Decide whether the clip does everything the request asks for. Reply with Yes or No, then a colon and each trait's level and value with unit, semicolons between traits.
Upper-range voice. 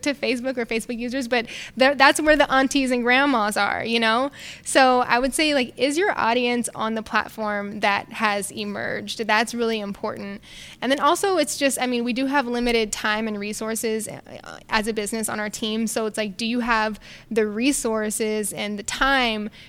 Yes: high, 230 Hz